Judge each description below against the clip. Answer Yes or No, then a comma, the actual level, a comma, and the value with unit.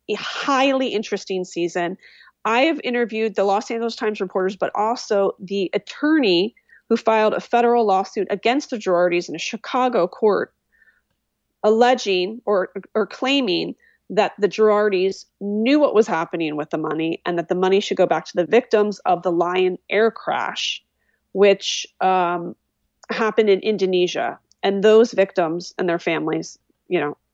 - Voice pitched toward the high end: Yes, high, 200 Hz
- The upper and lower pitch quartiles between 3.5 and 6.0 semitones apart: Yes, average, 3.8 semitones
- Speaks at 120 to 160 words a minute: Yes, average, 155 wpm